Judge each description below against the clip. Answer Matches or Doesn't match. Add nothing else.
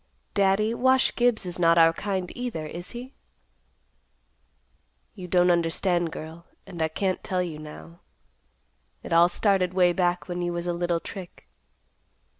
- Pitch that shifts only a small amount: Matches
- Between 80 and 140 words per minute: Doesn't match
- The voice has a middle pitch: Matches